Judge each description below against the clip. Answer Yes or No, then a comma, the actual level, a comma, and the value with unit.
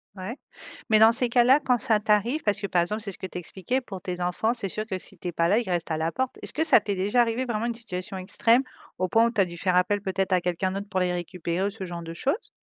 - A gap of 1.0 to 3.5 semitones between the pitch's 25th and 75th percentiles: No, average, 4.1 semitones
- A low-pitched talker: No, high, 200 Hz